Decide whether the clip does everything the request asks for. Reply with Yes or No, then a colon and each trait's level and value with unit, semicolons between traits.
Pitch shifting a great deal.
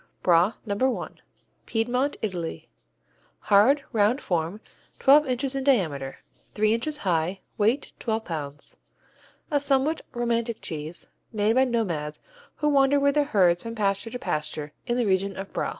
Yes: wide, 6.6 semitones